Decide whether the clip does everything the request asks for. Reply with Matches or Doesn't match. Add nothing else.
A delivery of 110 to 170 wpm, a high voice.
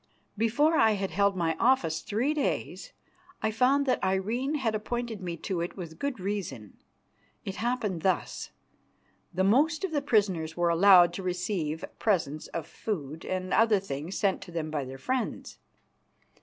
Matches